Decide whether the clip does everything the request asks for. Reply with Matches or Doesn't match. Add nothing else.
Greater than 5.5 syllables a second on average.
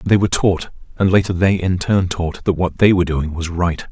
Doesn't match